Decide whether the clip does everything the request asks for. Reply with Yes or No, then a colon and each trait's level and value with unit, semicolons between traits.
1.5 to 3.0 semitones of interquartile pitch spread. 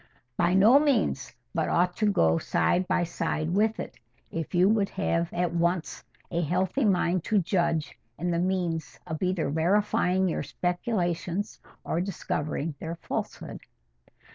Yes: narrow, 2.4 semitones